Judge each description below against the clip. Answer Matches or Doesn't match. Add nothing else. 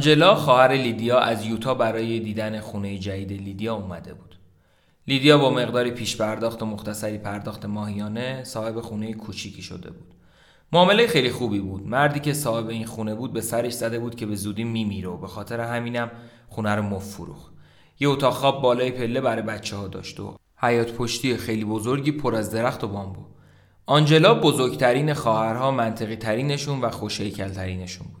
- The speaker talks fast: Matches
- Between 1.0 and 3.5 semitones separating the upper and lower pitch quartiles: Matches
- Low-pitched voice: Matches